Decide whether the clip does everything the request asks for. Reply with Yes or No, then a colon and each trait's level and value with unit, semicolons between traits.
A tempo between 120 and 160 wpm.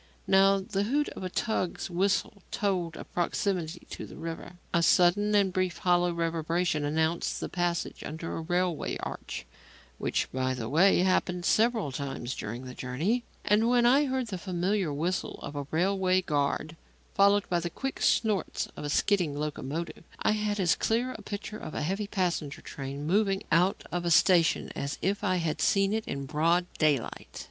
No: average, 175 wpm